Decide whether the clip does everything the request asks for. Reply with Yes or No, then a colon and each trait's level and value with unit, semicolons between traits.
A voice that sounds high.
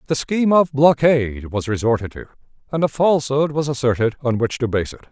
No: low, 135 Hz